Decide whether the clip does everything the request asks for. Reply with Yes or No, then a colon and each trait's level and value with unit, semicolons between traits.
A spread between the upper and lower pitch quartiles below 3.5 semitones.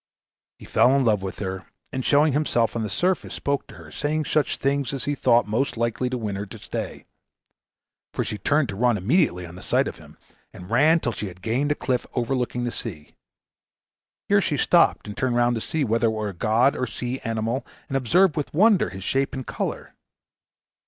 No: average, 4.5 semitones